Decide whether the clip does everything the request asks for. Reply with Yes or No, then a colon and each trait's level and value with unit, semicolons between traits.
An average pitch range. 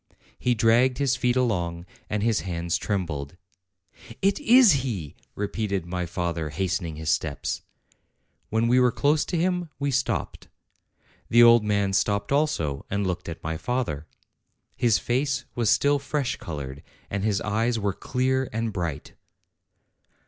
No: wide, 6.6 semitones